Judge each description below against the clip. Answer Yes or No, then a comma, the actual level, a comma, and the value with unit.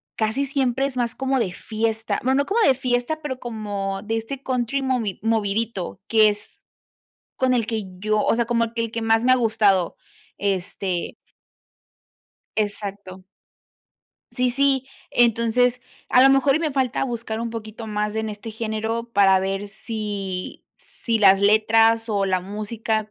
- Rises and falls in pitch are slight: No, average, 3.0 semitones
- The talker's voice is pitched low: No, high, 225 Hz